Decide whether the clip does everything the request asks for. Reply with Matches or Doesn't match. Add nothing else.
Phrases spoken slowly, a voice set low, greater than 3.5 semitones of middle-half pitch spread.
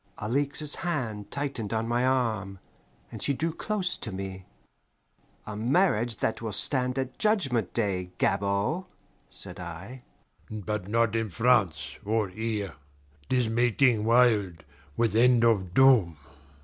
Matches